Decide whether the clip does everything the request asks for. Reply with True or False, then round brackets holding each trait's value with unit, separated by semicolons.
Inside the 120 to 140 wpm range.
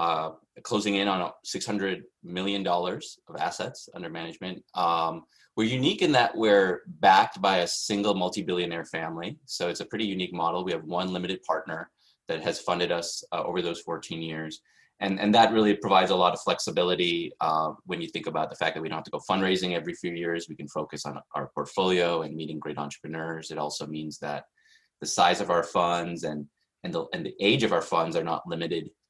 False (205 wpm)